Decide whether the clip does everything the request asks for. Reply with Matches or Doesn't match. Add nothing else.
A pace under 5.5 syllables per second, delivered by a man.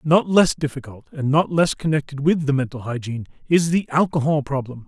Doesn't match